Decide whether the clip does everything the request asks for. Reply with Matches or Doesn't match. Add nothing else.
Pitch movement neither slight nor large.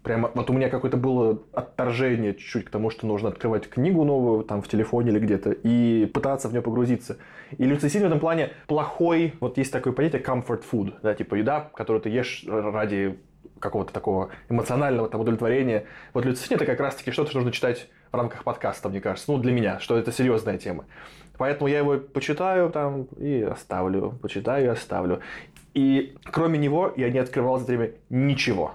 Matches